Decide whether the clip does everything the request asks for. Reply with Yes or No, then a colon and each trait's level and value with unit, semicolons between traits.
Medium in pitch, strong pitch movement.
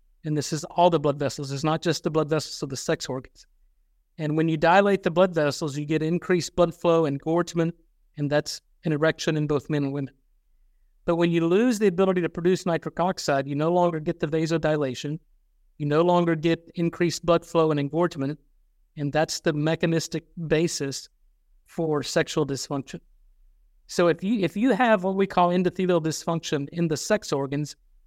No: medium, 160 Hz; average, 2.8 semitones